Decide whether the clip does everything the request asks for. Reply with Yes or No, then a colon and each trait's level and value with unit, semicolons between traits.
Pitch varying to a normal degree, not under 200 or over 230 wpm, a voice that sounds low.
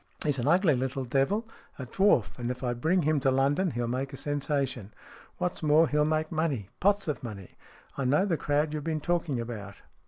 No: average, 4.0 semitones; fast, 205 wpm; medium, 145 Hz